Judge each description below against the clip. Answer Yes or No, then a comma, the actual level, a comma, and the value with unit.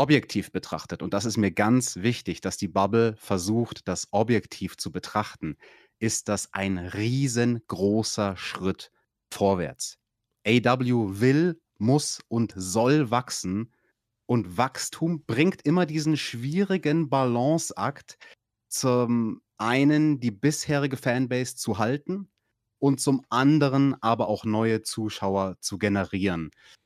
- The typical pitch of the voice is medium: No, low, 120 Hz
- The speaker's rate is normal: No, slow, 115 wpm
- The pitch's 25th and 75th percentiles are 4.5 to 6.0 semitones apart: Yes, average, 5.1 semitones